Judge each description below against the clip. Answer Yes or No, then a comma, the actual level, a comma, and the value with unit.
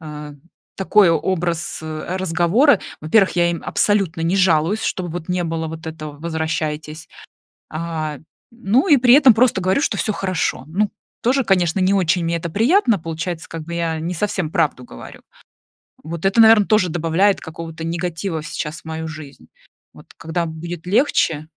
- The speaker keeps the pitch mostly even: No, average, 3.3 semitones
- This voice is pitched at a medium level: Yes, medium, 170 Hz